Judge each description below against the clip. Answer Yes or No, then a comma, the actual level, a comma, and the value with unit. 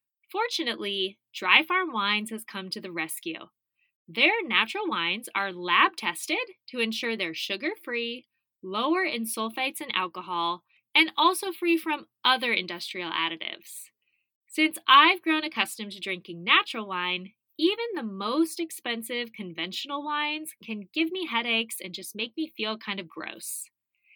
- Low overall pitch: No, high, 230 Hz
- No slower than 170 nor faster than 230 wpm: No, average, 145 wpm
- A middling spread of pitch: No, wide, 8.5 semitones